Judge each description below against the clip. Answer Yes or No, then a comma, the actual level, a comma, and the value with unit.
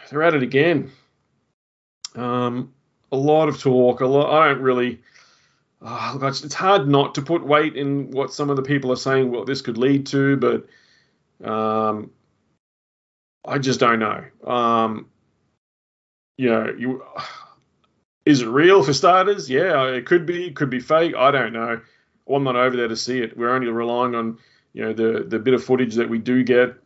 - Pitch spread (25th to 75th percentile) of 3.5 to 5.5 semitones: No, average, 3.0 semitones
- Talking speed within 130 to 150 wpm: No, average, 180 wpm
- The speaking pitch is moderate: No, low, 130 Hz